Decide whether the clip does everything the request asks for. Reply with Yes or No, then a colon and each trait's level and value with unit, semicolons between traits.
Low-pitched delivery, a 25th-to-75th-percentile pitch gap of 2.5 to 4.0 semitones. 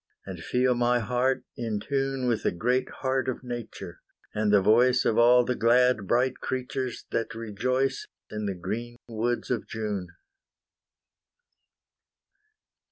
Yes: low, 120 Hz; average, 2.8 semitones